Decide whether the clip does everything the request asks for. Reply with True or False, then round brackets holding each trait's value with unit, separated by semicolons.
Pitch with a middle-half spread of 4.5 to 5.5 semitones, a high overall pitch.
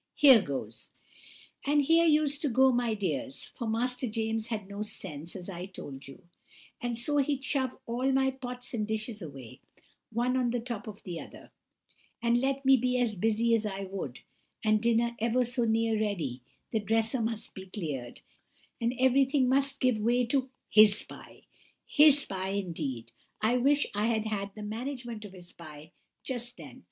False (4.1 semitones; 230 Hz)